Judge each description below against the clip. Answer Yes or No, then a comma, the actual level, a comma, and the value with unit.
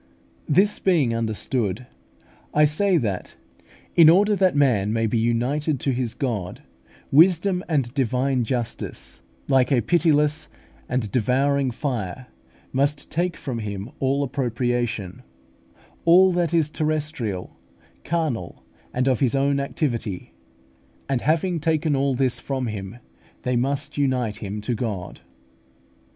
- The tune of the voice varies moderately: Yes, average, 4.6 semitones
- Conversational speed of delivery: No, slow, 125 wpm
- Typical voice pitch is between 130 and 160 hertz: Yes, low, 135 Hz